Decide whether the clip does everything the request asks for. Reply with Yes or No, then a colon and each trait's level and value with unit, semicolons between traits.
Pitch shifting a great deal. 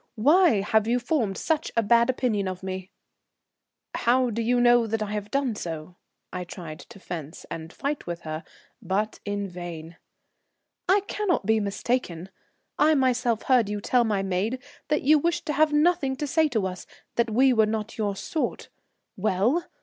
Yes: wide, 5.7 semitones